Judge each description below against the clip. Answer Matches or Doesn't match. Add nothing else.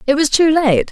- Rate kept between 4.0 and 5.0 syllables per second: Matches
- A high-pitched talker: Matches